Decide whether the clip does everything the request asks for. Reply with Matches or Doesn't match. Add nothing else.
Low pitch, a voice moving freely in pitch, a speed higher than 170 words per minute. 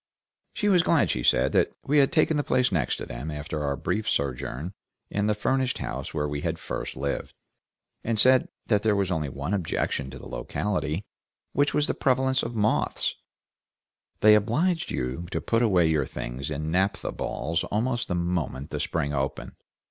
Matches